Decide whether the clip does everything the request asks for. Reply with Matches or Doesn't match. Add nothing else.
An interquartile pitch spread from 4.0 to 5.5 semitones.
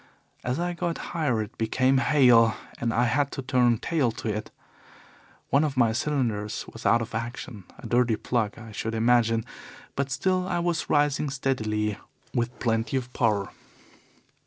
Doesn't match